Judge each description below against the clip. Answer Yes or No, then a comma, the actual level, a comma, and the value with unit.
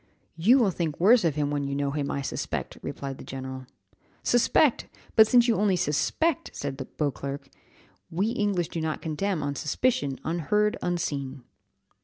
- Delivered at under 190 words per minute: Yes, average, 160 wpm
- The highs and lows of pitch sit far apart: Yes, wide, 6.8 semitones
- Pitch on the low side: No, medium, 160 Hz